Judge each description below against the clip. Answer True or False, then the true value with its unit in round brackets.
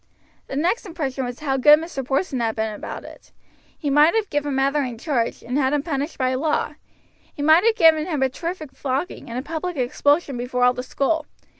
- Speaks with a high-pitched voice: True (285 Hz)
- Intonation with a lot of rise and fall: False (3.6 semitones)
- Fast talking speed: True (210 wpm)